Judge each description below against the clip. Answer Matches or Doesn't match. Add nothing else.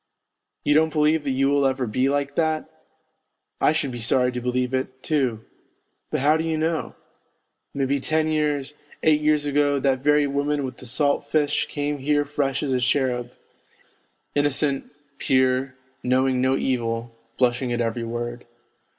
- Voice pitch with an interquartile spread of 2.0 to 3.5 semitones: Matches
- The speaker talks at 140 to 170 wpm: Matches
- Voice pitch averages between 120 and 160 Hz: Matches